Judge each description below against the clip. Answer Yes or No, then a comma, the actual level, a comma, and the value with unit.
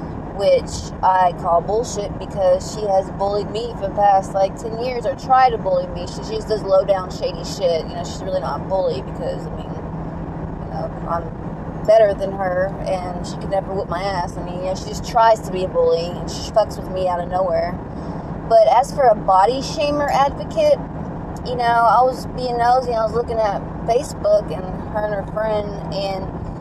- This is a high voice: Yes, high, 195 Hz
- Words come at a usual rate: No, fast, 210 wpm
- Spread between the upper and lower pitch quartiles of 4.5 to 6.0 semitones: No, average, 3.9 semitones